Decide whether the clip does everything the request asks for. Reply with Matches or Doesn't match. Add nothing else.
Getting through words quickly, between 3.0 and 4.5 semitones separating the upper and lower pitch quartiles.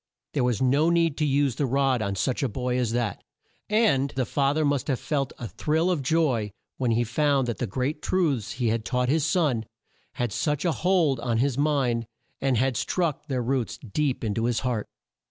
Matches